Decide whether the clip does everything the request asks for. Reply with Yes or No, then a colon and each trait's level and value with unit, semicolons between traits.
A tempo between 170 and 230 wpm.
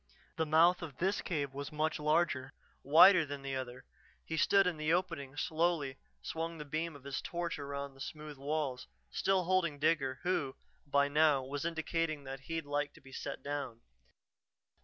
Yes: average, 175 wpm